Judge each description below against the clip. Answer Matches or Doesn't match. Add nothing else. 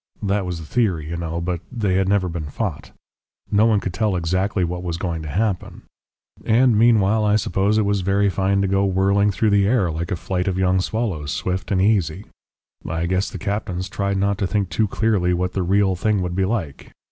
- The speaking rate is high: Matches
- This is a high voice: Doesn't match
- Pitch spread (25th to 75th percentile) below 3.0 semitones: Matches